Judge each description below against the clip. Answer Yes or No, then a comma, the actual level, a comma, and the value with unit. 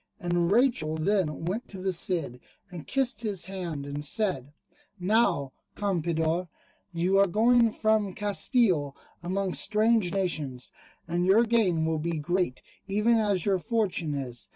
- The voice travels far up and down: No, average, 4.5 semitones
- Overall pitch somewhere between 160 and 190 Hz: Yes, medium, 185 Hz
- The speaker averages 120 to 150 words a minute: Yes, average, 140 wpm